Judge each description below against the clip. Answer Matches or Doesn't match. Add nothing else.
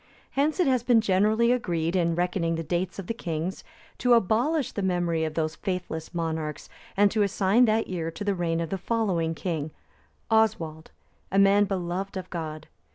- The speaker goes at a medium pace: Matches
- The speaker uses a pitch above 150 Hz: Matches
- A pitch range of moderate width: Matches